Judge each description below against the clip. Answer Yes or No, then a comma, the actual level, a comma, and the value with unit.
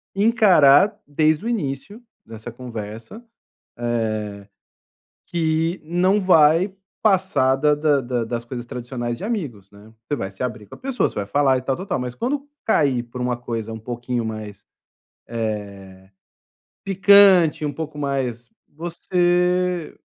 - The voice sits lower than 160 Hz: Yes, medium, 140 Hz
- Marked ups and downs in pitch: Yes, wide, 7.1 semitones